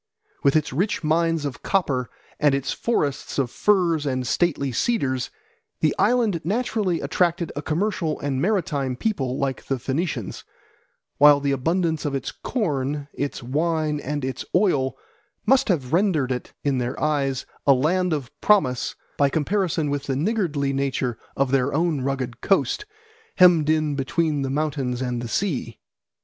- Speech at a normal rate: Yes, average, 155 wpm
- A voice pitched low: No, medium, 145 Hz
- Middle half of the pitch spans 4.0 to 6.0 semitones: Yes, average, 4.3 semitones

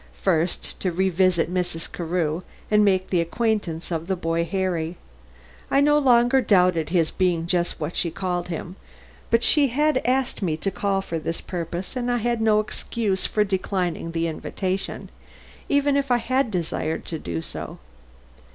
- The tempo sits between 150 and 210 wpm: Yes, average, 165 wpm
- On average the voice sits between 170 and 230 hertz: Yes, medium, 185 Hz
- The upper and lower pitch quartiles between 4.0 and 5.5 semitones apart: Yes, average, 5.0 semitones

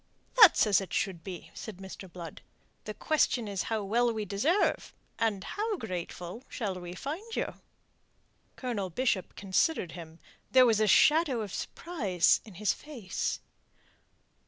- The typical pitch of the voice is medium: No, high, 210 Hz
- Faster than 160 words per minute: No, average, 145 wpm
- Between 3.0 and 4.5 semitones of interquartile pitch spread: No, wide, 5.6 semitones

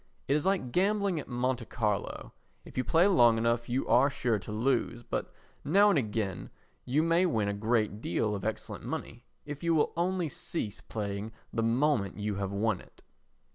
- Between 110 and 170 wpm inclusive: No, average, 185 wpm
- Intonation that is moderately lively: No, wide, 6.1 semitones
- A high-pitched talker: No, low, 120 Hz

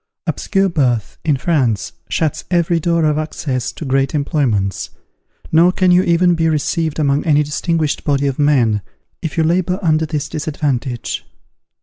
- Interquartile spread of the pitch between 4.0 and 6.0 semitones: No, average, 3.2 semitones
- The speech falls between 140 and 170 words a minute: Yes, average, 155 wpm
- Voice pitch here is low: No, medium, 155 Hz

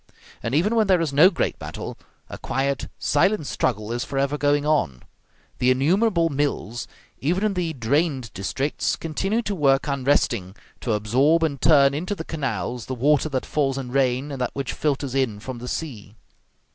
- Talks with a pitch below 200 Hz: Yes, medium, 140 Hz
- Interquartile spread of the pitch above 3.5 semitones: Yes, average, 4.0 semitones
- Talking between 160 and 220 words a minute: Yes, average, 175 wpm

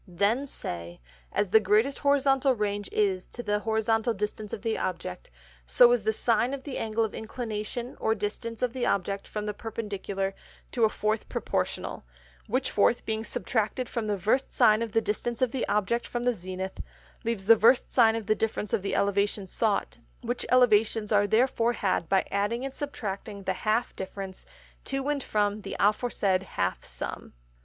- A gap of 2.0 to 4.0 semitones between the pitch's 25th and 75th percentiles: Yes, average, 2.9 semitones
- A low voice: No, high, 220 Hz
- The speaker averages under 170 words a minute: No, average, 180 wpm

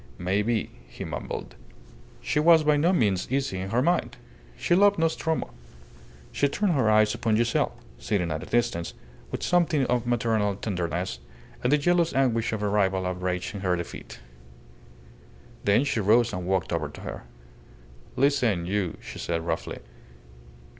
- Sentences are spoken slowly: No, average, 160 wpm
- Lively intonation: Yes, wide, 7.1 semitones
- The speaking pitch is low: Yes, low, 110 Hz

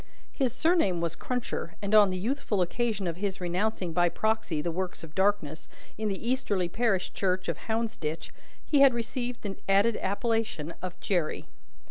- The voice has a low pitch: No, high, 200 Hz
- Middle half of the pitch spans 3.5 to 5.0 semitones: Yes, average, 4.3 semitones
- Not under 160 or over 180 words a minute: Yes, average, 165 wpm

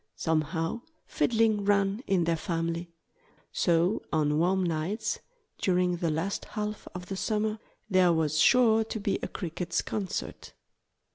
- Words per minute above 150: No, slow, 135 wpm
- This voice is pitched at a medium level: Yes, medium, 180 Hz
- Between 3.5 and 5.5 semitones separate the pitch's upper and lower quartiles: Yes, average, 4.0 semitones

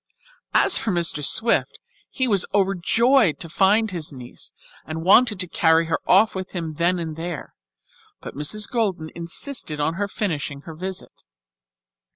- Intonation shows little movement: No, average, 4.1 semitones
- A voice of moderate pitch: Yes, medium, 175 Hz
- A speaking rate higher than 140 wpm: Yes, average, 155 wpm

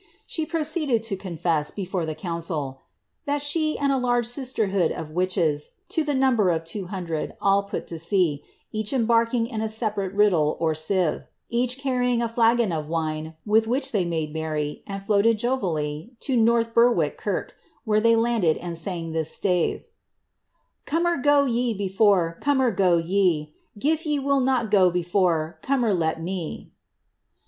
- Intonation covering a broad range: Yes, wide, 6.4 semitones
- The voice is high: Yes, high, 200 Hz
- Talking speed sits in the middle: Yes, average, 170 wpm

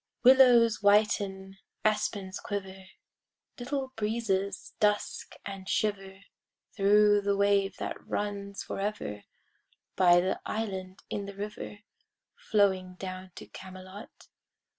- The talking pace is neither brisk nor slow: No, slow, 100 wpm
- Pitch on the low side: No, high, 200 Hz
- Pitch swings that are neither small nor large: No, narrow, 1.7 semitones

